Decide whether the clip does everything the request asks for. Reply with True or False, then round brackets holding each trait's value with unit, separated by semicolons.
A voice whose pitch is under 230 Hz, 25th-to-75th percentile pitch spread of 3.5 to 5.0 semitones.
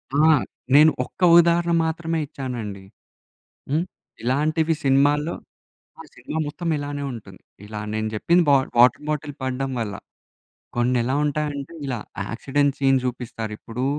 True (140 Hz; 3.8 semitones)